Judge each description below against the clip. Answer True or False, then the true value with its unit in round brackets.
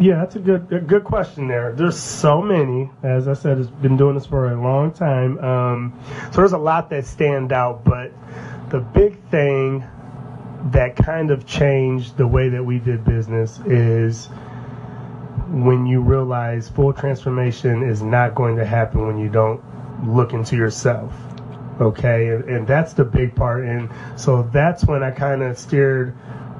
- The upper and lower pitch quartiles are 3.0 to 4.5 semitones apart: False (2.5 semitones)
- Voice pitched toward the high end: False (130 Hz)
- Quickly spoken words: False (170 wpm)